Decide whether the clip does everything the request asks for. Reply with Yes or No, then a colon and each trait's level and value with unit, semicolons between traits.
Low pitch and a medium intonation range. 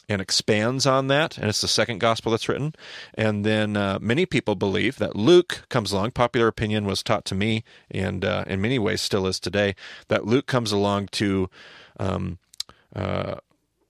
Yes: low, 110 Hz; average, 3.4 semitones